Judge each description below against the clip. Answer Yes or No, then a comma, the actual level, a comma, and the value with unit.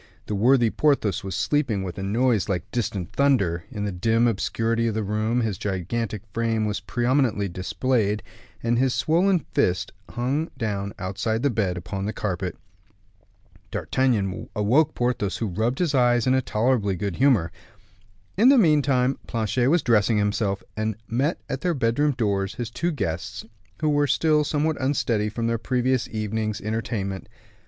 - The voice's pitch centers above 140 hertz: No, low, 115 Hz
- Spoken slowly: No, average, 160 wpm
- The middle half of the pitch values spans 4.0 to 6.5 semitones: Yes, average, 4.4 semitones